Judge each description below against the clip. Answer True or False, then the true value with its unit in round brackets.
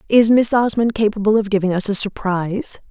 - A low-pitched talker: False (210 Hz)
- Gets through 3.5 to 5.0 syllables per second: False (5.6 syllables/s)